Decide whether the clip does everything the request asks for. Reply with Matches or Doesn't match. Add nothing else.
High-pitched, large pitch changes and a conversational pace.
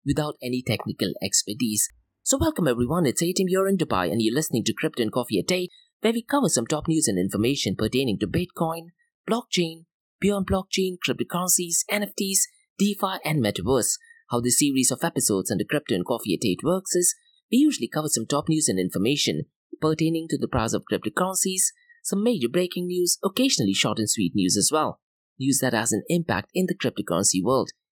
Doesn't match